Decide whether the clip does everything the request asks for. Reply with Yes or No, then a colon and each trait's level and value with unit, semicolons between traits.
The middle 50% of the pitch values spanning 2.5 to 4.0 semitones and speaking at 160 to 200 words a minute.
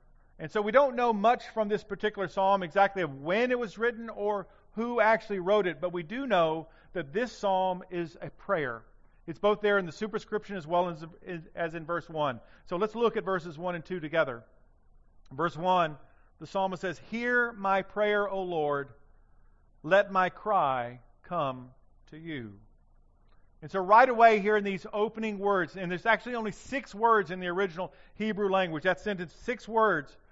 No: average, 4.5 semitones; average, 185 wpm